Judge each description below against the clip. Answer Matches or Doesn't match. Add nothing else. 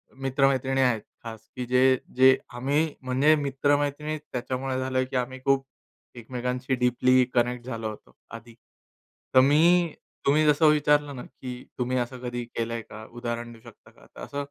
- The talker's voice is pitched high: Doesn't match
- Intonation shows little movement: Matches